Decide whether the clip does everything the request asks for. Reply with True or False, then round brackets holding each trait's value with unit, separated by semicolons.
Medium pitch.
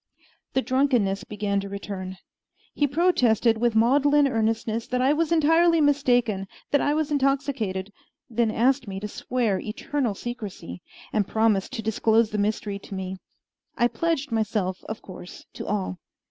False (225 Hz)